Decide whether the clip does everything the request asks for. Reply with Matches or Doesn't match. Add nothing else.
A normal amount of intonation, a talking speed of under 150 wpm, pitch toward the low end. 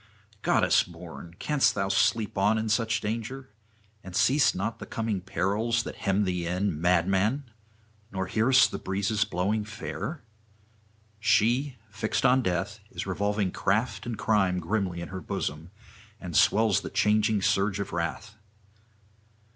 Matches